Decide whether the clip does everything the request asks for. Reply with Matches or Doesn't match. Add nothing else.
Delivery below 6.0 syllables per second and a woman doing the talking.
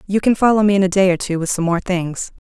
Doesn't match